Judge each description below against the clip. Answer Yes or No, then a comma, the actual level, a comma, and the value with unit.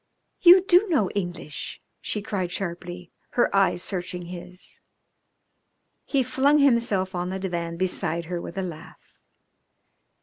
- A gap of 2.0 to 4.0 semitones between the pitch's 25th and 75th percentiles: No, average, 4.8 semitones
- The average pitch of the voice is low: No, medium, 185 Hz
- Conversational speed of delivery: No, slow, 130 wpm